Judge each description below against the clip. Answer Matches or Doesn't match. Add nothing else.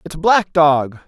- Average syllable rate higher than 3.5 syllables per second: Doesn't match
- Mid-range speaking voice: Matches